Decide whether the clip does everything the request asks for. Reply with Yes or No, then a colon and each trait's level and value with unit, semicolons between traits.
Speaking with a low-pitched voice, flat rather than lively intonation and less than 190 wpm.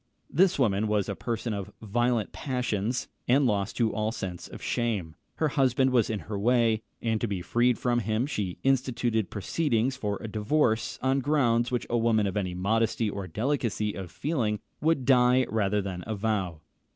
No: low, 115 Hz; average, 3.4 semitones; average, 175 wpm